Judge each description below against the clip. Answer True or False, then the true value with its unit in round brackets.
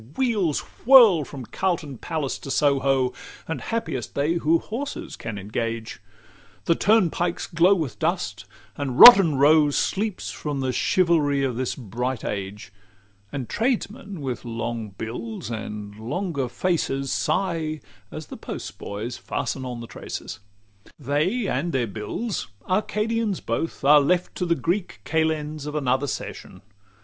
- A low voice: False (145 Hz)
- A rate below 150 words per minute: True (140 wpm)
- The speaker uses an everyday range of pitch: False (6.3 semitones)